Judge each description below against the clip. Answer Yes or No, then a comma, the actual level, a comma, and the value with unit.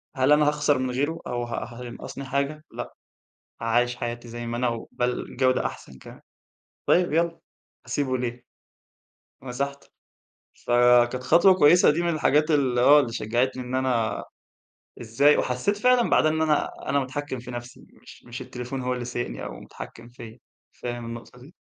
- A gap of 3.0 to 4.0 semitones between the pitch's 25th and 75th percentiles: Yes, average, 3.3 semitones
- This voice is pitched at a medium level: No, low, 125 Hz